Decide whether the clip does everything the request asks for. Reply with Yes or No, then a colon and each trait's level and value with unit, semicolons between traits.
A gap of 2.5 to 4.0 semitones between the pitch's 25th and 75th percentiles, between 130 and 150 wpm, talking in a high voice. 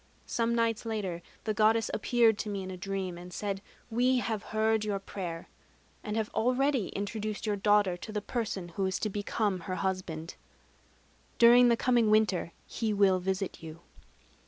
No: average, 2.9 semitones; average, 170 wpm; high, 210 Hz